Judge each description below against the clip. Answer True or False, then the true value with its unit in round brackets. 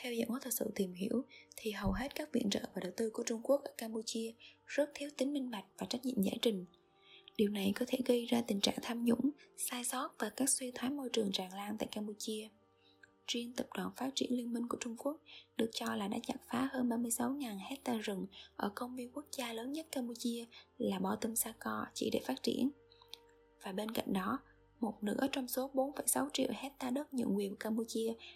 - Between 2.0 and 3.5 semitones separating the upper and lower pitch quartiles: True (2.9 semitones)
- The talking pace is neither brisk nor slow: True (220 wpm)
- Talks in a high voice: True (245 Hz)